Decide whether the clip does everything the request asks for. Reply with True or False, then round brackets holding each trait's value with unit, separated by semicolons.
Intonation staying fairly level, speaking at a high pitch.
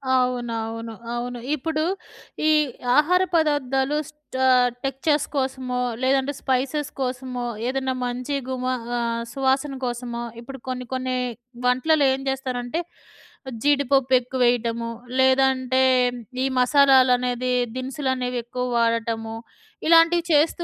True (1.8 semitones; 260 Hz)